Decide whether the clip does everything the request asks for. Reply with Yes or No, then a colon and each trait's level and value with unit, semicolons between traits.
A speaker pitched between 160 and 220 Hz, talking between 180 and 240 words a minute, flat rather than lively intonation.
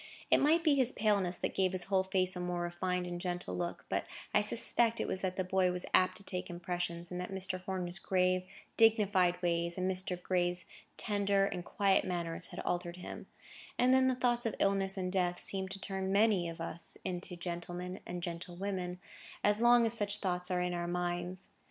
Yes: medium, 185 Hz; average, 200 wpm; narrow, 1.9 semitones